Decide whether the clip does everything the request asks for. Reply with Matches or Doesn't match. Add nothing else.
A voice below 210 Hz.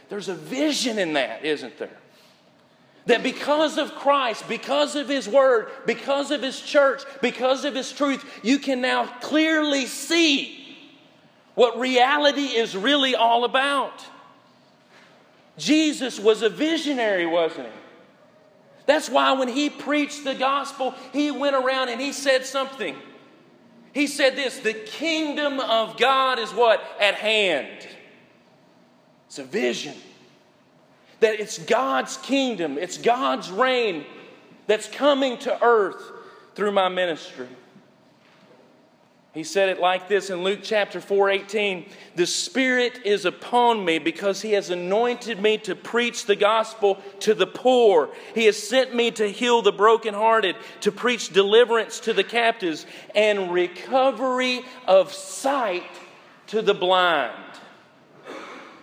Doesn't match